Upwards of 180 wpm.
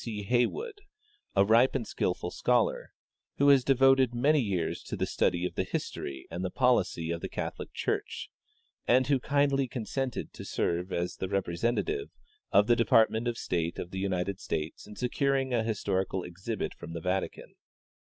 No: average, 170 wpm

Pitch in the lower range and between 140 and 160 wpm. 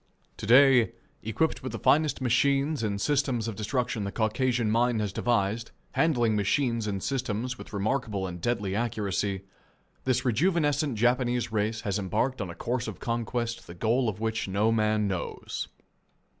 Yes: low, 115 Hz; average, 155 wpm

